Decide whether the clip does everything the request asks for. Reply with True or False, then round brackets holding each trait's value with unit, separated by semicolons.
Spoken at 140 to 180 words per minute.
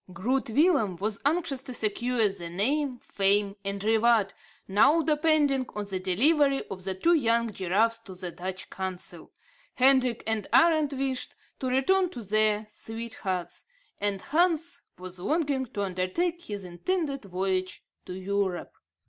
True (145 wpm)